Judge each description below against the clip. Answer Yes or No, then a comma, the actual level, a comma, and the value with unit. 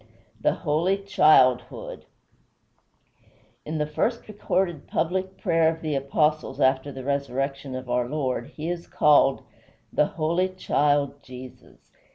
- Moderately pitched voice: Yes, medium, 150 Hz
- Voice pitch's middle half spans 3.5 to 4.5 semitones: Yes, average, 3.8 semitones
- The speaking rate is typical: No, slow, 130 wpm